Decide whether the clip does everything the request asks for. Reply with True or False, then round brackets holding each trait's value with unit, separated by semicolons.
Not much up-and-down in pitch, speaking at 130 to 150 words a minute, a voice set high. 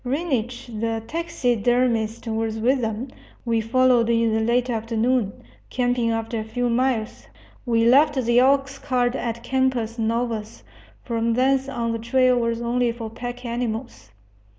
True (1.9 semitones; 140 wpm; 235 Hz)